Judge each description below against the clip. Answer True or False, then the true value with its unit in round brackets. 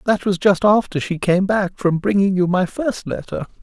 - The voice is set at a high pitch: True (195 Hz)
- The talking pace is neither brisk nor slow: False (215 wpm)